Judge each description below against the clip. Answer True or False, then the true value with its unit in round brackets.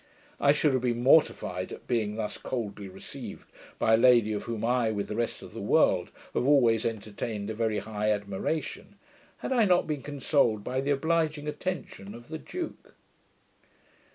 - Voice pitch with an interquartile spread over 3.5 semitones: True (5.2 semitones)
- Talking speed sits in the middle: True (175 wpm)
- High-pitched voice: False (120 Hz)